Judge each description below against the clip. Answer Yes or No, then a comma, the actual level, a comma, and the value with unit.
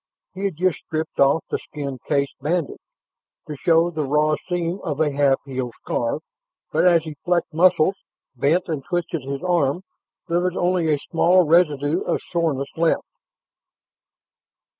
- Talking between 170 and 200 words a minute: No, average, 155 wpm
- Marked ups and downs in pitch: No, average, 3.6 semitones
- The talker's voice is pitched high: No, medium, 160 Hz